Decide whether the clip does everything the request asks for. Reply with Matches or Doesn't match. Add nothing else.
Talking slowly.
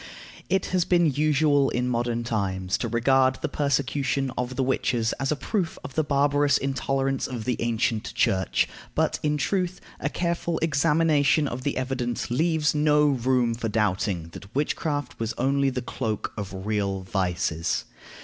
Doesn't match